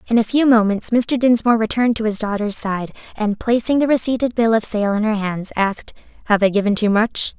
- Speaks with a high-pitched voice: Yes, high, 220 Hz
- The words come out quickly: Yes, fast, 220 wpm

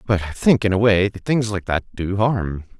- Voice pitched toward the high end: No, low, 100 Hz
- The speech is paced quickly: Yes, fast, 235 wpm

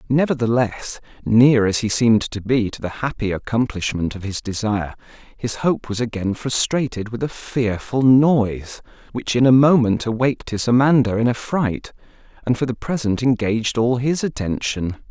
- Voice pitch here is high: No, low, 120 Hz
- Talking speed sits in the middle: Yes, average, 165 wpm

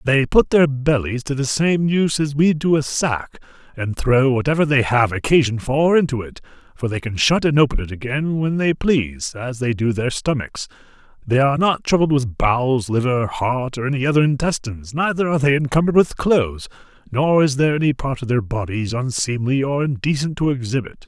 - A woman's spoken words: No, male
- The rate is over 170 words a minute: Yes, average, 195 wpm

